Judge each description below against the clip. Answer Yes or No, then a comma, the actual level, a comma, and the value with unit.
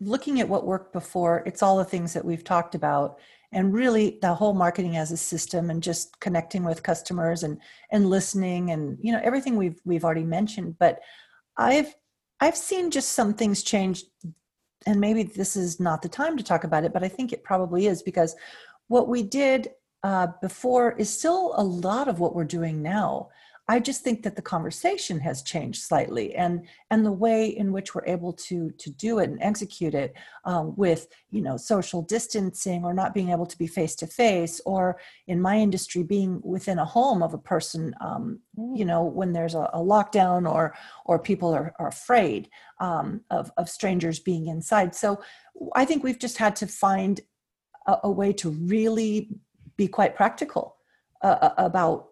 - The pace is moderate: Yes, average, 190 wpm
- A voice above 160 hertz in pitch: Yes, high, 190 Hz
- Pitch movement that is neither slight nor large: Yes, average, 4.1 semitones